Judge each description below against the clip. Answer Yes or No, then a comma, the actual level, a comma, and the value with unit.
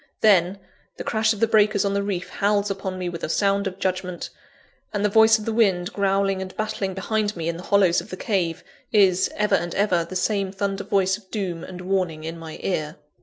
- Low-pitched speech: No, high, 195 Hz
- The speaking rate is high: Yes, fast, 220 wpm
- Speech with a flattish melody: Yes, narrow, 2.2 semitones